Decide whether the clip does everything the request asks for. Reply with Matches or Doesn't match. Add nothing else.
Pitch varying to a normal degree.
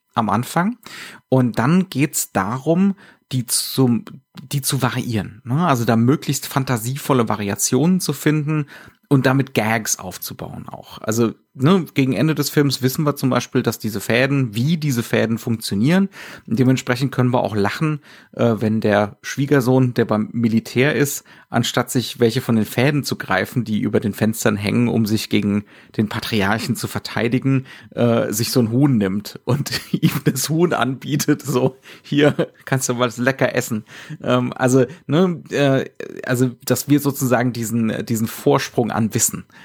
Matches